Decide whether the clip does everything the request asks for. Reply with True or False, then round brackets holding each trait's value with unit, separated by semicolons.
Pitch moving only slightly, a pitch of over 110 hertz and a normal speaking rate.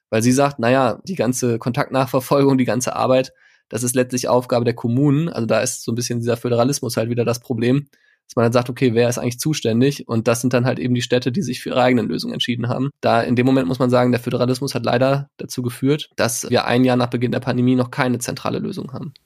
False (1.5 semitones; 125 Hz; 250 wpm)